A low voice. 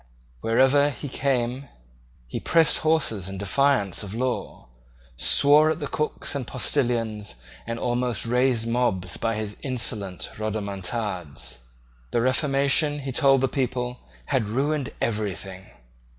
Yes: low, 120 Hz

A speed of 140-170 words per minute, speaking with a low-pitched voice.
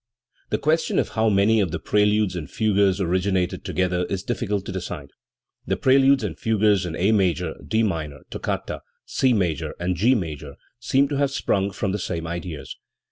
No: average, 180 wpm; very low, 95 Hz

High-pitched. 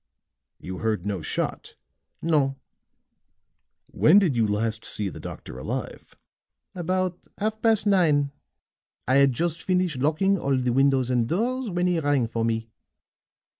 No: medium, 140 Hz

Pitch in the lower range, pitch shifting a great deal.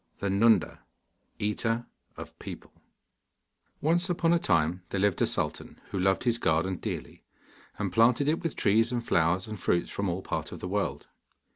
No: low, 105 Hz; average, 4.4 semitones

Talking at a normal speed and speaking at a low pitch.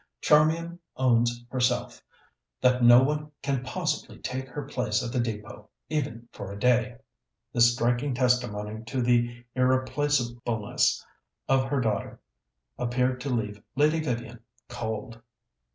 No: slow, 125 wpm; low, 125 Hz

